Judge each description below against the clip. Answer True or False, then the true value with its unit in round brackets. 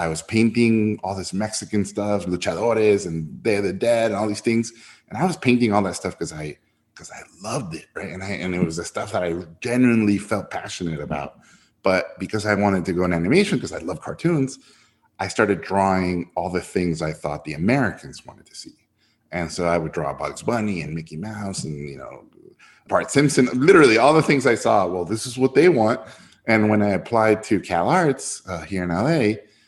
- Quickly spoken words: True (215 wpm)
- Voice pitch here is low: True (100 Hz)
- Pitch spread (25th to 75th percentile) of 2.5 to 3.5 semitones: False (4.4 semitones)